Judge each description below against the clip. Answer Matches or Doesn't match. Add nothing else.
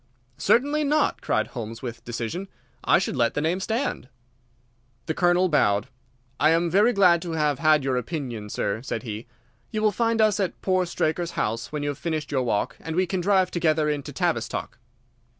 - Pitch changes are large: Matches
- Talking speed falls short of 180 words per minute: Doesn't match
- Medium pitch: Matches